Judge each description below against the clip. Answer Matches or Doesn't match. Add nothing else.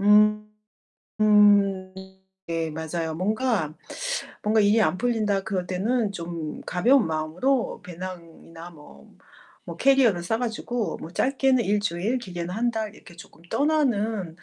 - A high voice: Matches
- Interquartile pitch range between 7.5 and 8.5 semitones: Doesn't match